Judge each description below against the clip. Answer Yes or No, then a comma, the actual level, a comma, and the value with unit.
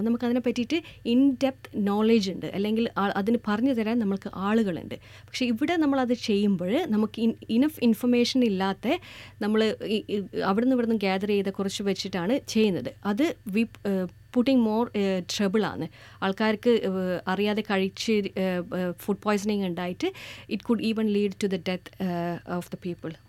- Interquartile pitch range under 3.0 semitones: No, average, 3.5 semitones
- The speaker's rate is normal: No, fast, 135 wpm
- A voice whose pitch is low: No, high, 210 Hz